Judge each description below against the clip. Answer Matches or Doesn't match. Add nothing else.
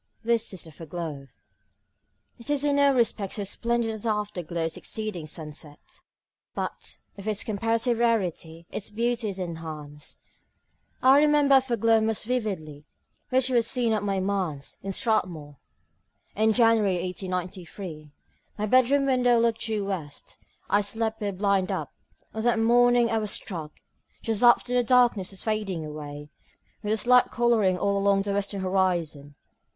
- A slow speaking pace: Doesn't match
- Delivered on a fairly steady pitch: Doesn't match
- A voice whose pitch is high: Matches